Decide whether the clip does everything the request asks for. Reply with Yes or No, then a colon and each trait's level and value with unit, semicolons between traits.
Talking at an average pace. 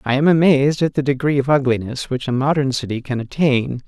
No: fast, 215 wpm